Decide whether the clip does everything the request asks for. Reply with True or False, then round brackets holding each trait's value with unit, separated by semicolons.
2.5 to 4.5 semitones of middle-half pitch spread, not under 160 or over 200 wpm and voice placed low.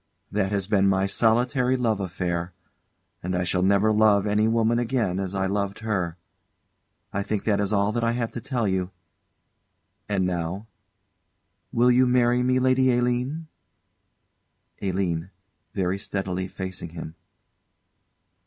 False (4.0 semitones; 140 wpm; 100 Hz)